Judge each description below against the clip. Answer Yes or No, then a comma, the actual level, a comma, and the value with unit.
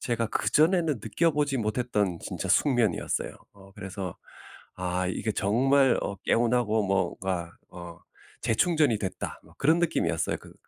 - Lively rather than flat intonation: Yes, wide, 6.1 semitones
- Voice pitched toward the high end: No, low, 110 Hz